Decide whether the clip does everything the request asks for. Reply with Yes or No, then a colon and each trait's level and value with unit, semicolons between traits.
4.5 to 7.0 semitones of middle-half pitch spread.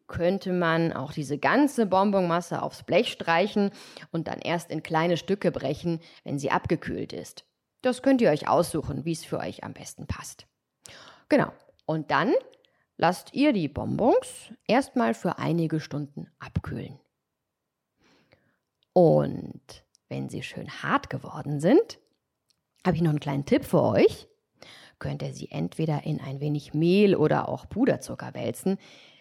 Yes: average, 4.9 semitones